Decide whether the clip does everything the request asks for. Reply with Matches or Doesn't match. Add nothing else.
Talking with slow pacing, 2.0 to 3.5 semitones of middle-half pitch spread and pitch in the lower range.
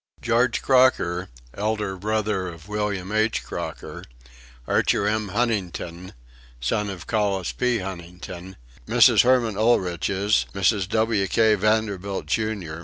Matches